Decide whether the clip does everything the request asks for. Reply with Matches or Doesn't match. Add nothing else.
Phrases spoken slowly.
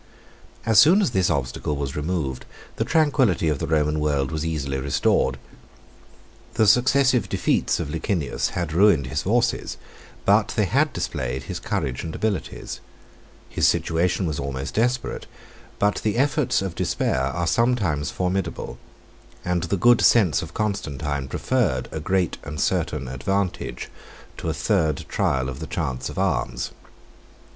Doesn't match